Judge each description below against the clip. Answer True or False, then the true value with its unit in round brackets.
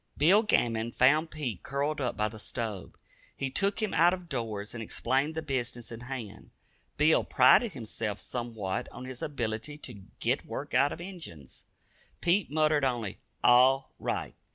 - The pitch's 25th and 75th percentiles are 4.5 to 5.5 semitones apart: True (5.2 semitones)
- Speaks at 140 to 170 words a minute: True (160 wpm)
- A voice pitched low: True (130 Hz)